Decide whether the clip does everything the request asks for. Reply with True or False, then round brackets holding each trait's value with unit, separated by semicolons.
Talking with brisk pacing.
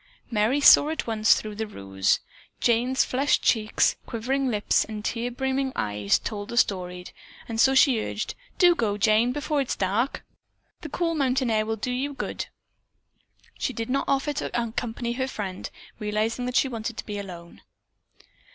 False (170 wpm)